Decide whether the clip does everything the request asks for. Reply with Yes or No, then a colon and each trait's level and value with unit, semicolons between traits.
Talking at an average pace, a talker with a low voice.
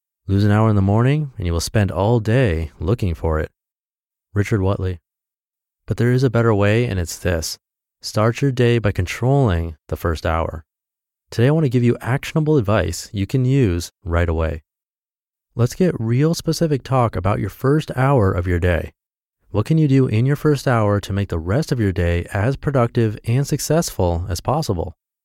Yes: average, 190 wpm; low, 110 Hz